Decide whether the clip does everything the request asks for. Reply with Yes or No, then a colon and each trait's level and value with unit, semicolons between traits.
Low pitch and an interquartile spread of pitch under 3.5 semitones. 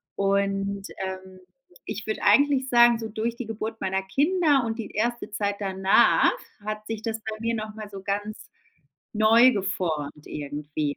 No: high, 215 Hz; average, 2.9 semitones